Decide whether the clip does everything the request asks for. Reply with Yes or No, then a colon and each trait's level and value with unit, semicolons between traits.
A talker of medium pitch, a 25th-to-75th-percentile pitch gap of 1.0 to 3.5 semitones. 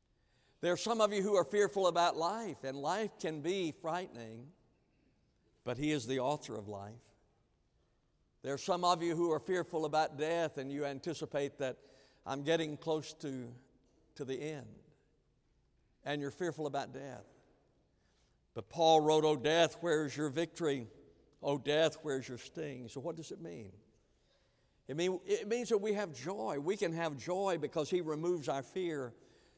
No: medium, 155 Hz; average, 4.2 semitones